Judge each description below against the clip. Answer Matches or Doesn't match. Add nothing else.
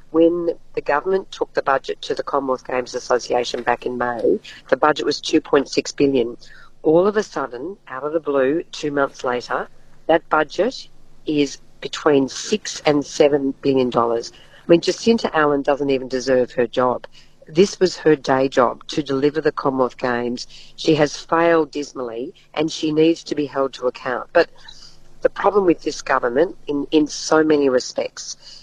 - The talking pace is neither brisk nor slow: Matches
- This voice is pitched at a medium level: Matches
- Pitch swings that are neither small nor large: Matches